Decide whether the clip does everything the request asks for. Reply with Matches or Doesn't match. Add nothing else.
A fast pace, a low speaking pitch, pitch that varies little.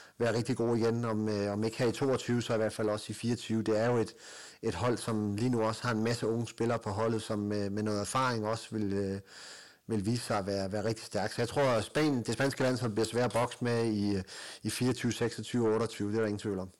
Matches